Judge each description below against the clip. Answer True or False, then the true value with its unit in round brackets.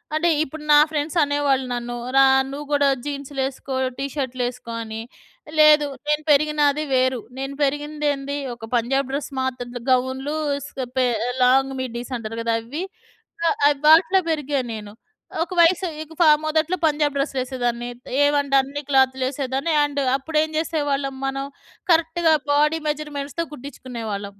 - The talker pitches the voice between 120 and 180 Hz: False (280 Hz)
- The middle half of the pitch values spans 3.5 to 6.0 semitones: False (2.5 semitones)